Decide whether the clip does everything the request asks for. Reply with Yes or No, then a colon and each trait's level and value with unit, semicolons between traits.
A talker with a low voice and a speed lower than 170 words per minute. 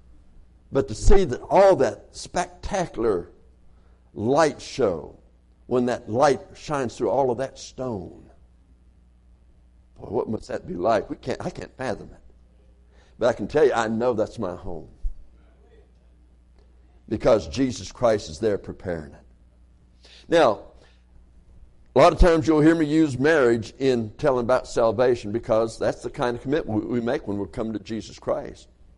Yes: very low, 85 Hz; average, 155 wpm